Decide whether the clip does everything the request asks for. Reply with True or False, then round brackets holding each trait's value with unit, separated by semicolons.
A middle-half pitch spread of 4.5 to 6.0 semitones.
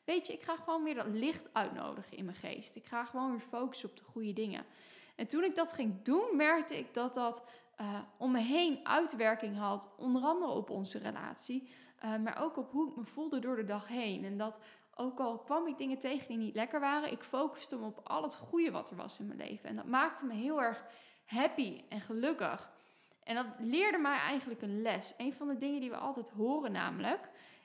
True (4.8 semitones)